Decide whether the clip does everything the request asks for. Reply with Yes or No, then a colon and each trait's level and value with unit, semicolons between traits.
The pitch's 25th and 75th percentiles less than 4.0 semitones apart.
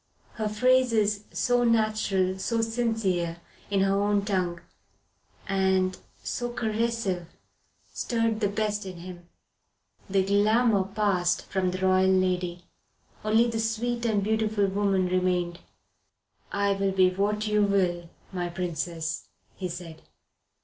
Yes: average, 2.9 semitones